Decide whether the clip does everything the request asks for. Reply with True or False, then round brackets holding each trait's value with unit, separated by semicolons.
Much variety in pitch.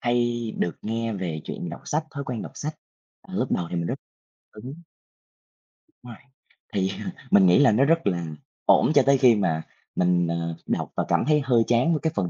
True (7.5 semitones)